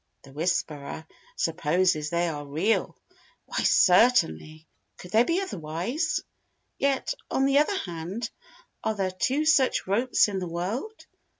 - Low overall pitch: No, medium, 185 Hz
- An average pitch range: No, wide, 8.1 semitones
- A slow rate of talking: Yes, slow, 130 wpm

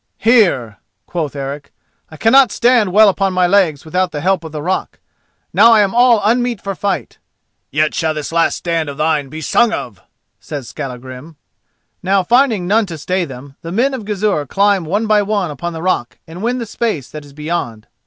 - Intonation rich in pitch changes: Yes, wide, 5.8 semitones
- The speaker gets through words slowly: No, average, 195 wpm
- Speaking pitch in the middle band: Yes, medium, 180 Hz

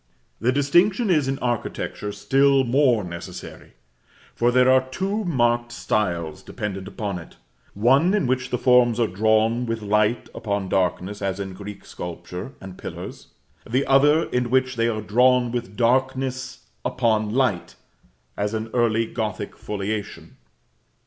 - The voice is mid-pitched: No, low, 115 Hz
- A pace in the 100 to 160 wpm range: Yes, average, 140 wpm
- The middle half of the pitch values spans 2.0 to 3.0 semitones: No, average, 4.1 semitones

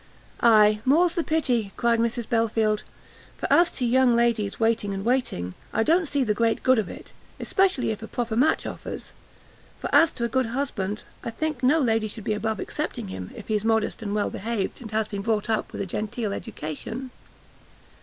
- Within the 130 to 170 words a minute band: No, average, 195 wpm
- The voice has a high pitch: Yes, high, 225 Hz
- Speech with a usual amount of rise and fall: Yes, average, 3.1 semitones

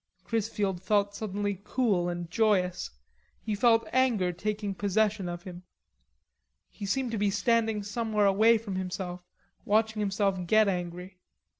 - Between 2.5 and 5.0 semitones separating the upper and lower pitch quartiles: Yes, average, 2.8 semitones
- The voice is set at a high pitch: Yes, high, 205 Hz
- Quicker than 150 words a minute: No, slow, 135 wpm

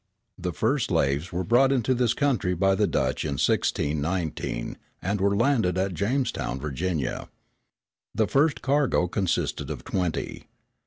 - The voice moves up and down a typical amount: No, wide, 6.4 semitones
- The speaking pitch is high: No, very low, 95 Hz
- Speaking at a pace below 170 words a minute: Yes, average, 140 wpm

